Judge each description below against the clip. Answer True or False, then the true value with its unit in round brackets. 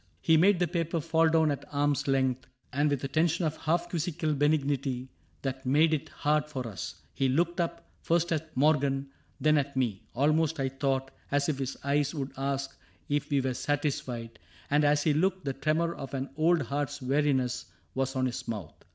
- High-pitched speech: False (145 Hz)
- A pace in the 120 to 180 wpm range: False (200 wpm)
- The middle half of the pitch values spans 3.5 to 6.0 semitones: False (2.9 semitones)